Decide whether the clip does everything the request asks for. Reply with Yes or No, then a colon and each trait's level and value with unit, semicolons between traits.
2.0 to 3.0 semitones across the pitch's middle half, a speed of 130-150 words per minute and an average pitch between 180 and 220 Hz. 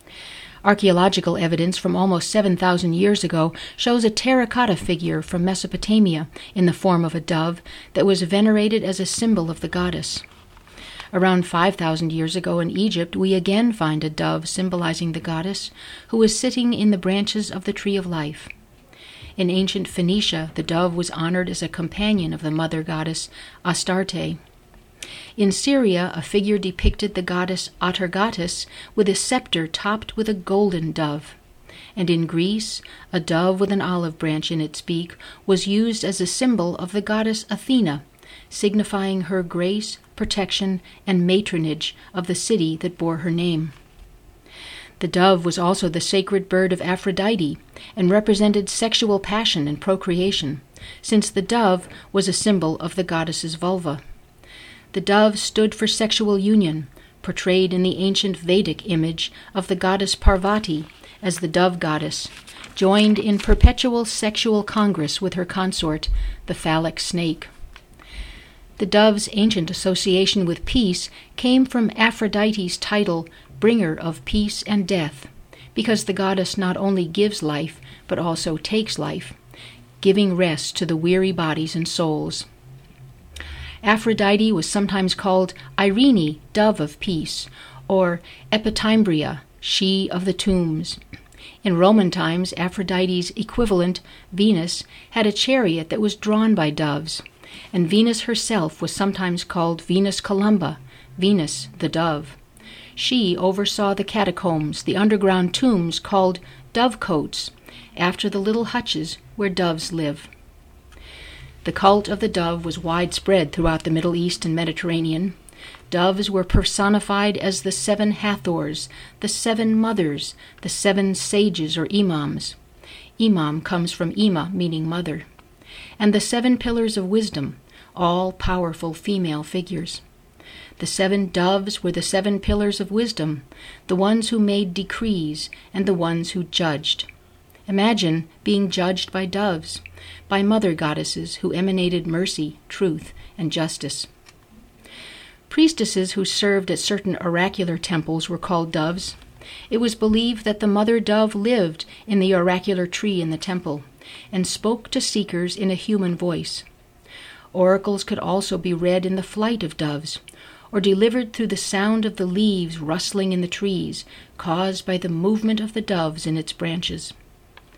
No: average, 3.7 semitones; average, 145 wpm; medium, 185 Hz